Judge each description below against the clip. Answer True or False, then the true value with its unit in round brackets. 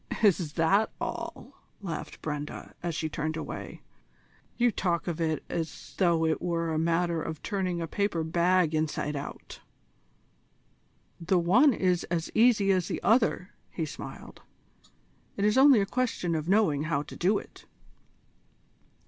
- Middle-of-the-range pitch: True (170 Hz)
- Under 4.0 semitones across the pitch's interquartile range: True (3.6 semitones)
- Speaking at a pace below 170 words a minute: True (150 wpm)